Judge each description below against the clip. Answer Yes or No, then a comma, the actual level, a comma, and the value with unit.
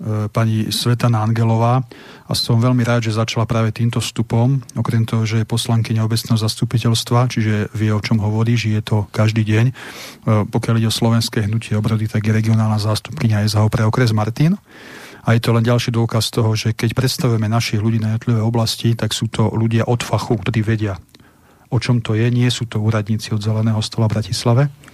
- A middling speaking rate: No, fast, 190 wpm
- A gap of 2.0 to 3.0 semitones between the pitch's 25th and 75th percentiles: No, narrow, 1.4 semitones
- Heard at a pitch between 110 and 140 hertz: Yes, low, 115 Hz